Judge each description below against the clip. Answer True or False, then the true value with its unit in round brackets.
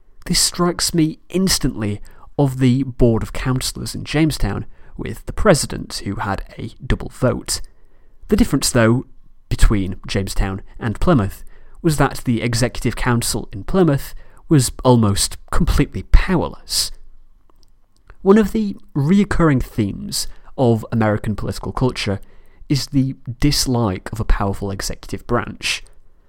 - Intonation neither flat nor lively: False (5.8 semitones)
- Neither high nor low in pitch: False (115 Hz)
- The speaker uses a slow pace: True (125 wpm)